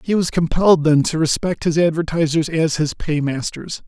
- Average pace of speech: Yes, average, 170 wpm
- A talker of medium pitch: Yes, medium, 160 Hz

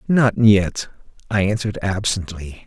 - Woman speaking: No, male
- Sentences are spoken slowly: Yes, slow, 110 wpm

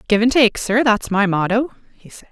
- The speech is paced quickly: Yes, fast, 235 wpm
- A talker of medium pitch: No, high, 220 Hz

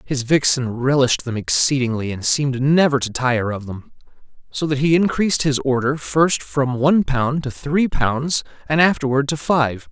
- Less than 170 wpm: No, average, 175 wpm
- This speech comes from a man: Yes, male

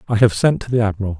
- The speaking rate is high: Yes, fast, 300 wpm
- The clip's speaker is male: Yes, male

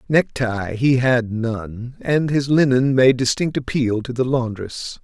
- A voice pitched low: Yes, low, 125 Hz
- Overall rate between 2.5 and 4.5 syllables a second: Yes, 3.8 syllables/s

